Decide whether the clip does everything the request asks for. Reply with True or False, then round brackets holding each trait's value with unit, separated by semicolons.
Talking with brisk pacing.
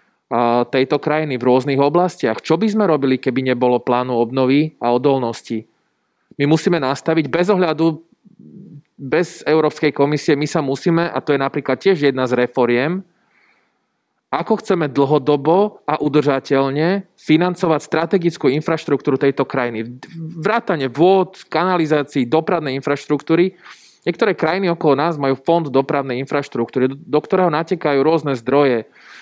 False (125 wpm)